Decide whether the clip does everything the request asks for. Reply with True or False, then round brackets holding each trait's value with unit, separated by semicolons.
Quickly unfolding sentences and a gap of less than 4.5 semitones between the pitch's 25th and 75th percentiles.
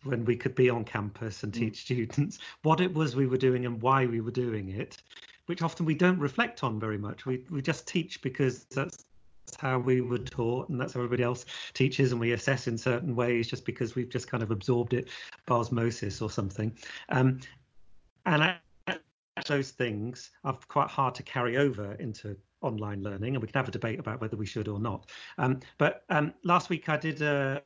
True (210 wpm; 2.9 semitones)